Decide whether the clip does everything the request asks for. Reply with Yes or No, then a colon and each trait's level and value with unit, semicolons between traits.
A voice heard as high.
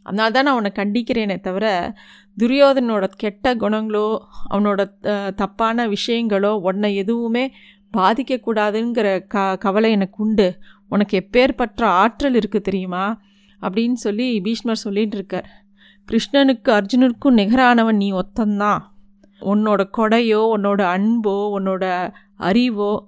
Yes: high, 210 Hz